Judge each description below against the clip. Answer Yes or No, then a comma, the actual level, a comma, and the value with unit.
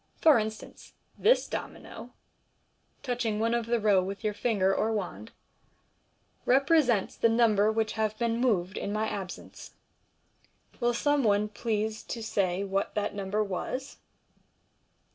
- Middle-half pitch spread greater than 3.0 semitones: No, narrow, 2.6 semitones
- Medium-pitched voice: No, high, 215 Hz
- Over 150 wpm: No, average, 145 wpm